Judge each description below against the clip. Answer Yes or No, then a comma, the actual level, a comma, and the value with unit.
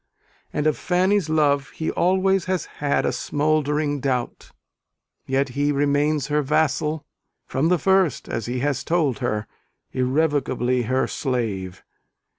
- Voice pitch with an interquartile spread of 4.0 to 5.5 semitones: No, average, 3.2 semitones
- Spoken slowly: Yes, slow, 130 wpm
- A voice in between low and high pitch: Yes, medium, 145 Hz